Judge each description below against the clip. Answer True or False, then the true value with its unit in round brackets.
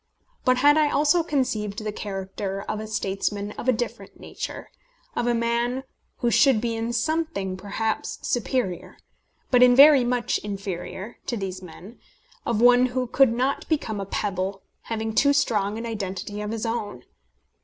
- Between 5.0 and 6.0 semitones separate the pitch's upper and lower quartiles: False (3.6 semitones)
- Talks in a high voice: True (225 Hz)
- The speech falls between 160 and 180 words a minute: True (165 wpm)